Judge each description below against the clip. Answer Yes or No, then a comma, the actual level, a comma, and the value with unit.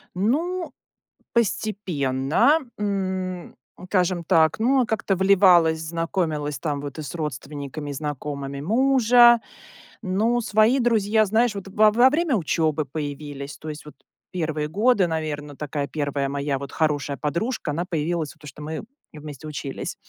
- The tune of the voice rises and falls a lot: Yes, wide, 6.2 semitones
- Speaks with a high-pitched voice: No, medium, 165 Hz